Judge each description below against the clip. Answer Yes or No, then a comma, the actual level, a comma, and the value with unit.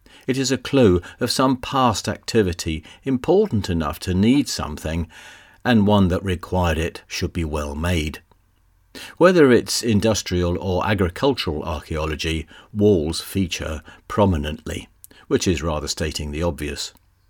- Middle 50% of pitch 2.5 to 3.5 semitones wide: No, average, 4.4 semitones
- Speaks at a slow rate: Yes, slow, 130 wpm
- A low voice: Yes, very low, 90 Hz